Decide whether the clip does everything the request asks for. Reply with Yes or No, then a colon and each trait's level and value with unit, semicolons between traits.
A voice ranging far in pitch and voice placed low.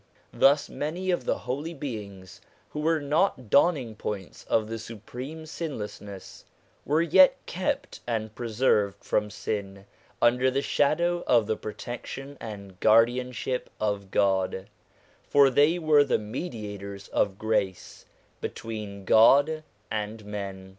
Yes: wide, 5.8 semitones; low, 115 Hz